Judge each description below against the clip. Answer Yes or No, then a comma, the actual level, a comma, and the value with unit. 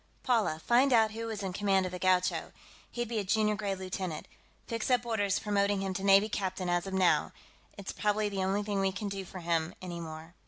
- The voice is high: Yes, high, 195 Hz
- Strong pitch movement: No, narrow, 2.5 semitones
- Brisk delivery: Yes, fast, 220 wpm